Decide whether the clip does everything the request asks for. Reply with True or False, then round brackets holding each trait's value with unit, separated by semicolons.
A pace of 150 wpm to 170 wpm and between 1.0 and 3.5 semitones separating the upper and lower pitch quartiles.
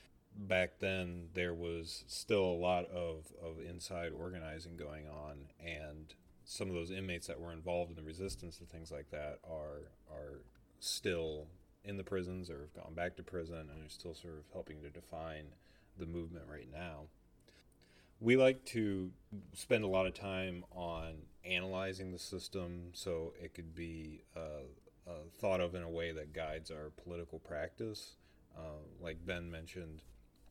True (165 wpm; 2.6 semitones)